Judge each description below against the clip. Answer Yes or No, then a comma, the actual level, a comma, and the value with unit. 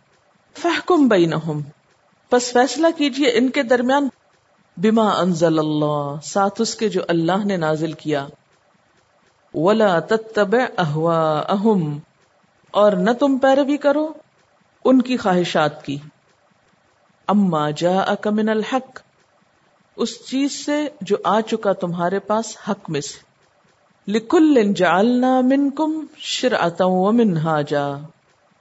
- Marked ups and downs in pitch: Yes, wide, 7.3 semitones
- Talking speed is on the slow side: Yes, slow, 105 wpm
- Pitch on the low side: No, high, 205 Hz